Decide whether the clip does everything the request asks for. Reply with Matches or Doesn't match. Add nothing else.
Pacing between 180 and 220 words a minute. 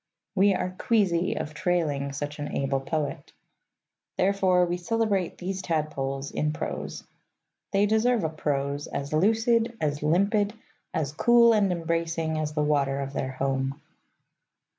Doesn't match